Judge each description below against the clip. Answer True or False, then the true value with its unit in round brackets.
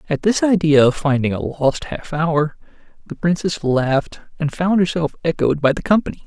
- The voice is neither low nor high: True (160 Hz)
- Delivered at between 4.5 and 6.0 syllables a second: True (5.1 syllables/s)